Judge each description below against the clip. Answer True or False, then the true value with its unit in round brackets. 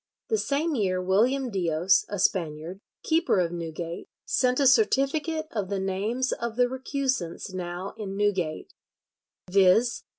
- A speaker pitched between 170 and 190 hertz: False (200 Hz)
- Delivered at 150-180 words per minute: False (135 wpm)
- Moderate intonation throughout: False (6.3 semitones)